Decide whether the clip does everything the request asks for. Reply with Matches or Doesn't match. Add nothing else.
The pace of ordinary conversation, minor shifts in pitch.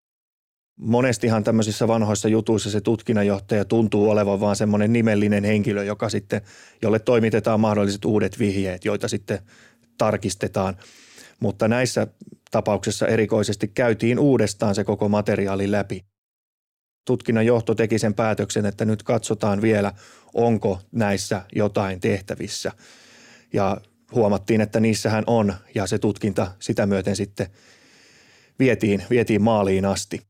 Matches